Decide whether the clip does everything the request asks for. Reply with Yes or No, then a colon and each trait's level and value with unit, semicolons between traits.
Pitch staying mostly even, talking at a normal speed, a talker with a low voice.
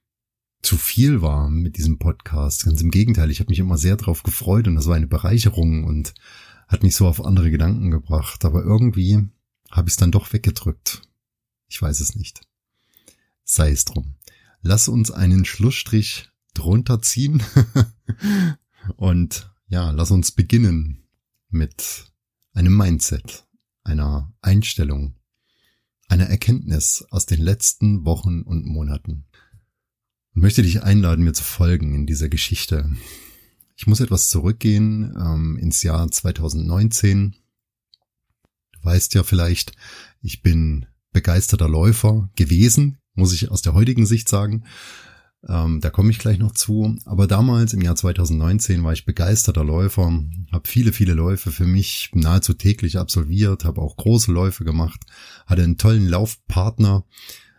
No: average, 4.3 semitones; average, 140 wpm; very low, 95 Hz